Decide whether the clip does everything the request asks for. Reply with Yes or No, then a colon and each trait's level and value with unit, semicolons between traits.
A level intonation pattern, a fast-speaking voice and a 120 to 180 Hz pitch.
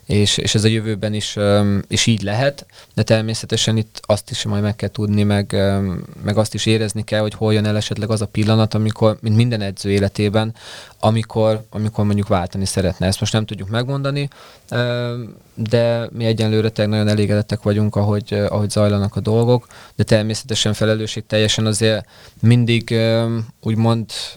No: narrow, 1.4 semitones; fast, 160 wpm; low, 110 Hz